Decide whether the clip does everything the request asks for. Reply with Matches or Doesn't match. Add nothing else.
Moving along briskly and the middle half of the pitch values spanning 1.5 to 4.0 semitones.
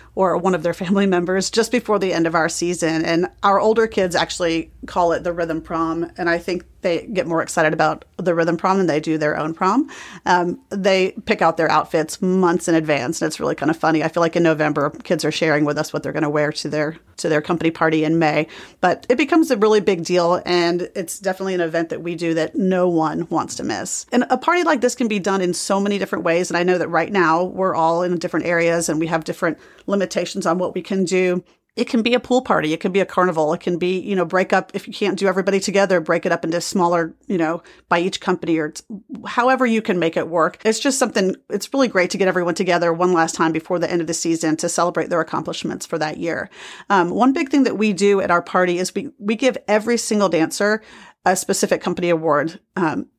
Matches